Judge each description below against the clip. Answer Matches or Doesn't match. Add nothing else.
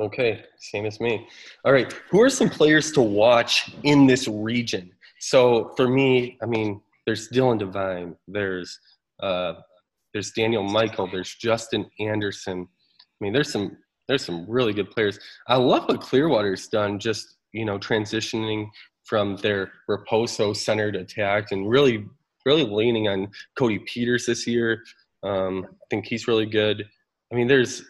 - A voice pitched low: Matches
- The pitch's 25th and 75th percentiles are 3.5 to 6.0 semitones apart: Doesn't match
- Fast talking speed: Doesn't match